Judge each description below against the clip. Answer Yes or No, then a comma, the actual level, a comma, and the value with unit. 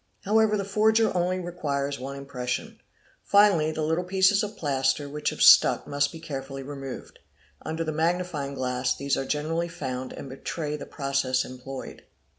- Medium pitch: Yes, medium, 150 Hz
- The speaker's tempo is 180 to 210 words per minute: No, average, 160 wpm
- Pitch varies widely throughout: No, average, 4.4 semitones